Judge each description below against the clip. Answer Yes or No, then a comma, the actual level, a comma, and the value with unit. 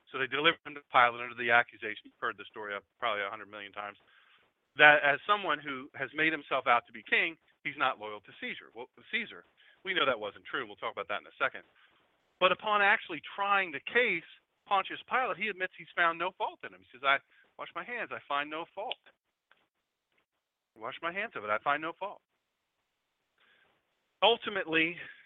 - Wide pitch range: Yes, wide, 7.5 semitones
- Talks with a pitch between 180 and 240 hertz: No, medium, 155 Hz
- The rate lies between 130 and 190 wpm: No, fast, 205 wpm